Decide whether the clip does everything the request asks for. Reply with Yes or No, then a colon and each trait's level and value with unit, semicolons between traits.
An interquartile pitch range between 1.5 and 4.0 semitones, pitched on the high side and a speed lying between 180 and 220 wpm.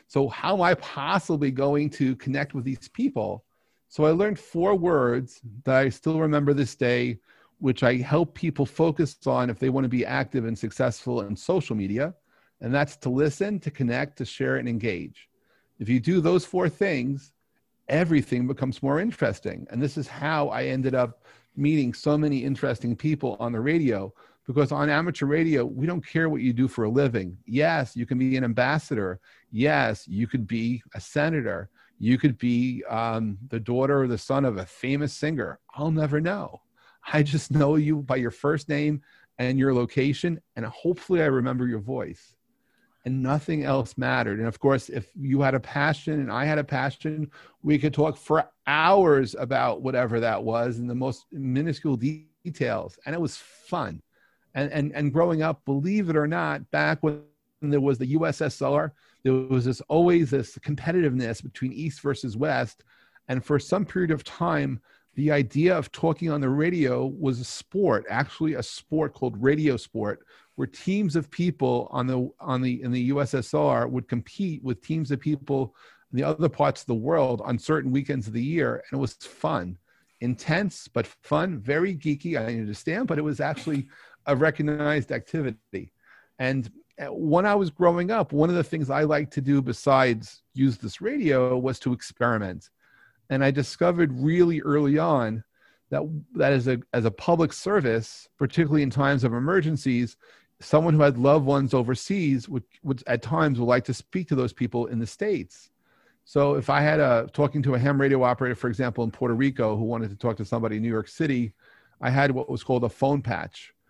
No: average, 3.5 semitones; medium, 140 Hz; average, 190 wpm